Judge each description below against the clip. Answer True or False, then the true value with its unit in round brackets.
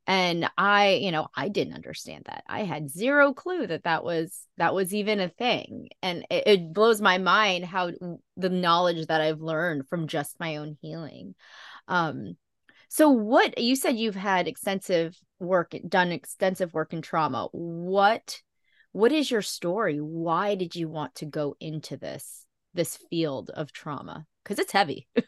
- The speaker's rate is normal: True (170 wpm)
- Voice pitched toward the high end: False (180 Hz)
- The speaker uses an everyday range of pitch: True (4.1 semitones)